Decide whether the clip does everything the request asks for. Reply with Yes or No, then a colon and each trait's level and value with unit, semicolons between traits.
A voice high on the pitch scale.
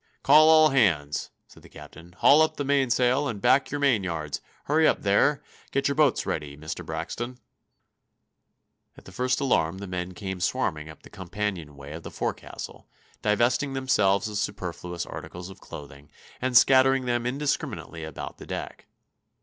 No: low, 105 Hz